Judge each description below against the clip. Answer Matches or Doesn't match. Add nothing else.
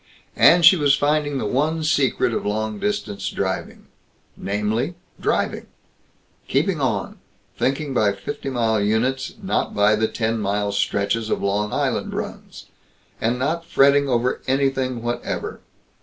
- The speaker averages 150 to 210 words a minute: Doesn't match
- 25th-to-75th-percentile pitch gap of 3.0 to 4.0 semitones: Doesn't match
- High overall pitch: Doesn't match